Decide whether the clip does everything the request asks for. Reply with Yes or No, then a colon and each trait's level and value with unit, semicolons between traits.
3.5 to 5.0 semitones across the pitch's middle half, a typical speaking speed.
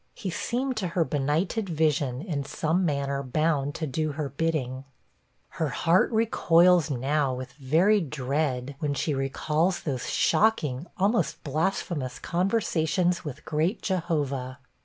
No: average, 4.2 semitones; slow, 130 wpm